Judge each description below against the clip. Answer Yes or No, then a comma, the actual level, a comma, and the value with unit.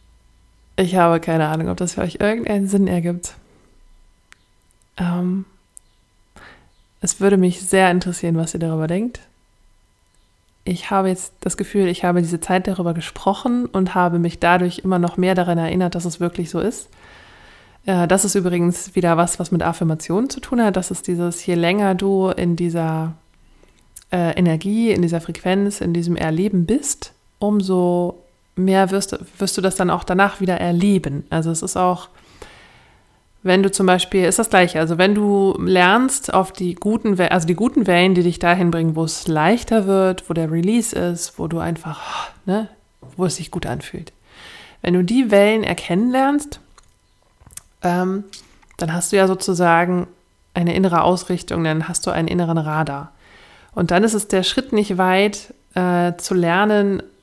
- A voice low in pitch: No, medium, 180 Hz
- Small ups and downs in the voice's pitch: Yes, narrow, 2.3 semitones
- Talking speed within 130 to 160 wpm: No, average, 170 wpm